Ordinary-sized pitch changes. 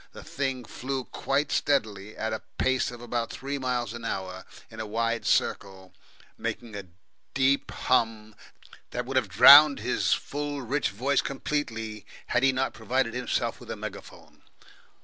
Yes: average, 3.5 semitones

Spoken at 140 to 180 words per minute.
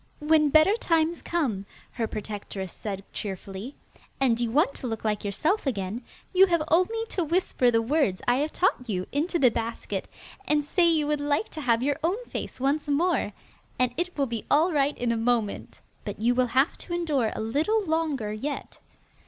No: average, 190 wpm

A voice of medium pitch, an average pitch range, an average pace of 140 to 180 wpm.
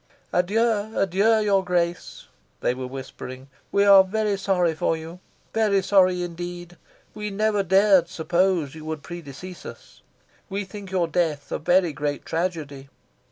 Yes: medium, 180 Hz; average, 3.5 semitones; average, 145 wpm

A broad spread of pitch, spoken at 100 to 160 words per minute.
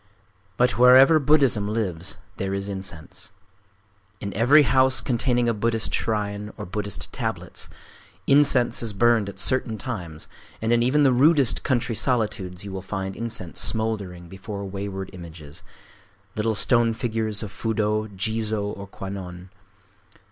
No: average, 3.4 semitones; slow, 135 wpm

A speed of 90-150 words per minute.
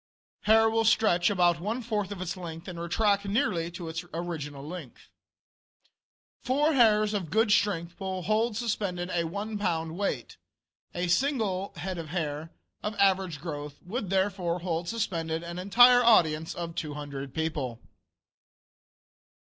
Yes: average, 140 wpm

